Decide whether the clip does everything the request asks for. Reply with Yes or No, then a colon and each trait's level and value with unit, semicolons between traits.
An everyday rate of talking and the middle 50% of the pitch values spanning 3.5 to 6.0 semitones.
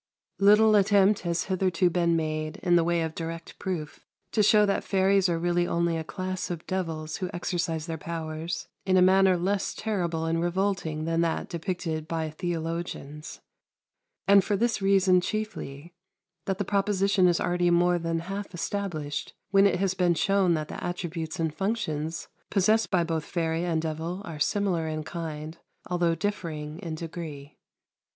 No: average, 165 wpm; average, 2.9 semitones